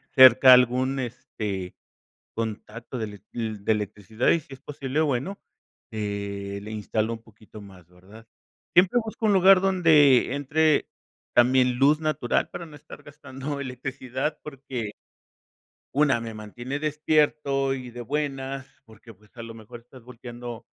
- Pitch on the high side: No, low, 125 Hz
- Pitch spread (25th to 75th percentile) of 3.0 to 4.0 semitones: No, average, 4.5 semitones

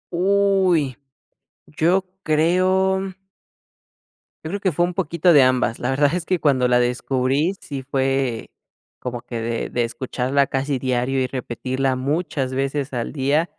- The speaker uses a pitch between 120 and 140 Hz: Yes, low, 135 Hz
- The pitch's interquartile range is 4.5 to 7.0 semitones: Yes, average, 4.9 semitones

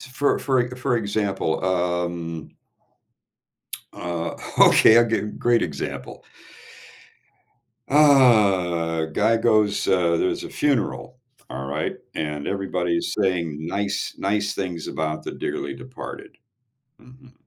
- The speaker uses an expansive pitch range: Yes, wide, 5.8 semitones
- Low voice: Yes, very low, 95 Hz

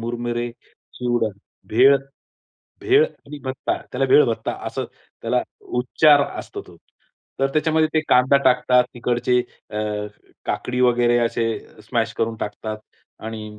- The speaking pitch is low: Yes, low, 125 Hz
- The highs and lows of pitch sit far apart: No, narrow, 2.5 semitones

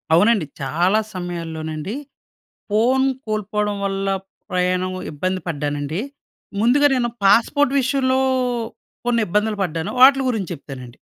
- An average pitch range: No, wide, 5.7 semitones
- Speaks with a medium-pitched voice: No, high, 195 Hz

